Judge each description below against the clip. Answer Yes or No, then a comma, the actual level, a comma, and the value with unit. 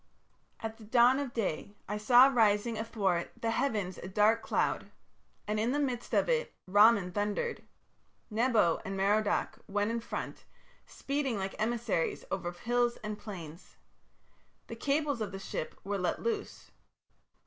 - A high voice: Yes, high, 215 Hz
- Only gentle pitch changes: No, average, 3.3 semitones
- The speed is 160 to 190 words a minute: No, average, 150 wpm